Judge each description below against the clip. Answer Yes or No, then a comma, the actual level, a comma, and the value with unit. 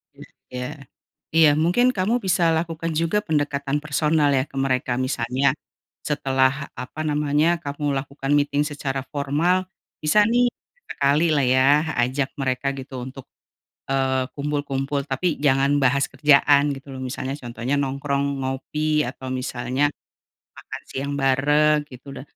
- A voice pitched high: No, medium, 140 Hz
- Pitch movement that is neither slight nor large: No, narrow, 2.2 semitones